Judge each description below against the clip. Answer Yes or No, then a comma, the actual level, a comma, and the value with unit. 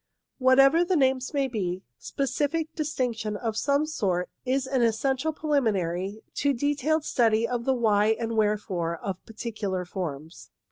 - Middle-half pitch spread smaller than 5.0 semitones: No, average, 5.3 semitones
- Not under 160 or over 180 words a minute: No, average, 145 wpm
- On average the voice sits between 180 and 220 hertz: No, high, 235 Hz